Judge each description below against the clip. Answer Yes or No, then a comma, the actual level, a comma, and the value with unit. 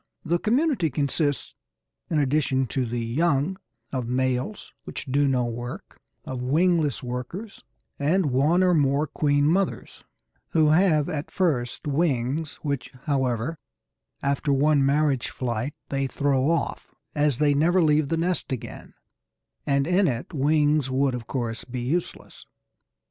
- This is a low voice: No, medium, 145 Hz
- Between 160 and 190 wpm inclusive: No, average, 140 wpm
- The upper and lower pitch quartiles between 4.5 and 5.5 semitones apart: No, average, 3.6 semitones